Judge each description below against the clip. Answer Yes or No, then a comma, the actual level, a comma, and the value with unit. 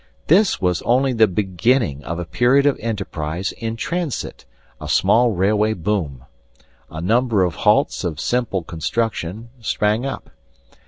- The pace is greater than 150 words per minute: No, average, 140 wpm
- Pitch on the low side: Yes, low, 105 Hz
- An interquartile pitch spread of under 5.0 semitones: No, wide, 5.5 semitones